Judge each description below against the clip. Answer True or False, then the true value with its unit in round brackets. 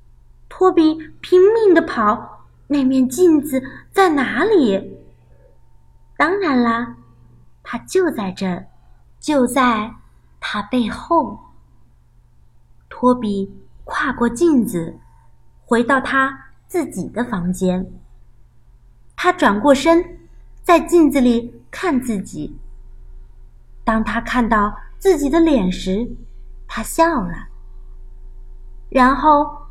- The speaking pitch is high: True (240 Hz)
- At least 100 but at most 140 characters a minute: True (130 characters per minute)